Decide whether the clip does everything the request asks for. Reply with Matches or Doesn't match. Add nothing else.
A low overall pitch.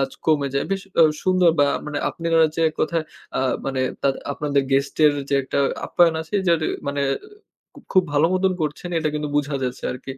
Doesn't match